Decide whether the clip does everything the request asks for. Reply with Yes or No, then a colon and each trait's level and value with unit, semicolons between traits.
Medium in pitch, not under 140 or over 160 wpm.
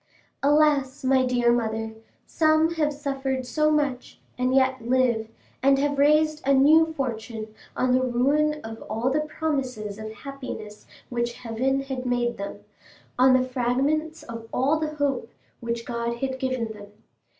No: very high, 260 Hz; average, 150 wpm